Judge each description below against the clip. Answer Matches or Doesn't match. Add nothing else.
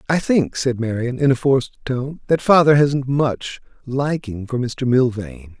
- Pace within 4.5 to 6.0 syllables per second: Doesn't match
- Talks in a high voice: Doesn't match